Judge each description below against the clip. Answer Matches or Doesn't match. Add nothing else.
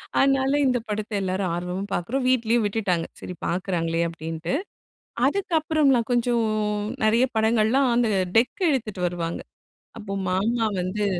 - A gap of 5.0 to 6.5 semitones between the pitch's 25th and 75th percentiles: Matches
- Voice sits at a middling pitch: Doesn't match